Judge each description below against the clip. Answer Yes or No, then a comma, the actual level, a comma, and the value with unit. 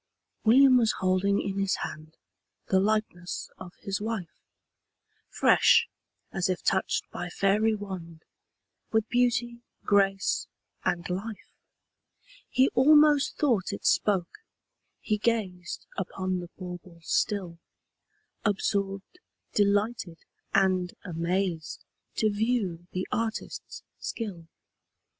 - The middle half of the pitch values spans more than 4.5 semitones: No, average, 3.5 semitones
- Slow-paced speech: Yes, slow, 100 wpm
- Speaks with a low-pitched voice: No, high, 195 Hz